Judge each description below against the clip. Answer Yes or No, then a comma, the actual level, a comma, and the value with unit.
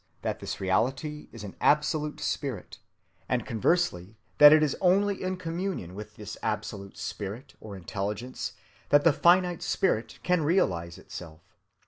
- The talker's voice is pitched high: No, low, 130 Hz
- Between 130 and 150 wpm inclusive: Yes, average, 140 wpm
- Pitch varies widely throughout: Yes, wide, 8.4 semitones